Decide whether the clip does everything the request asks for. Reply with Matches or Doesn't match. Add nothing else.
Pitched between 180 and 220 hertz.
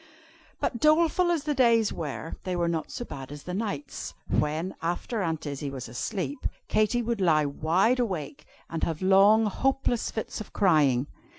Matches